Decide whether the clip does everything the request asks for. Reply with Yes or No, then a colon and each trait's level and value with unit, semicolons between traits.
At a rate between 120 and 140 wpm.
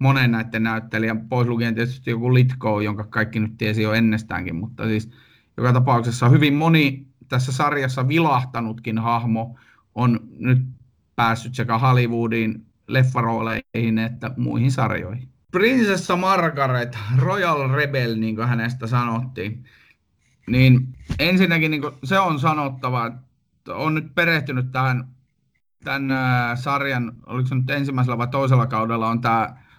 Yes: average, 130 wpm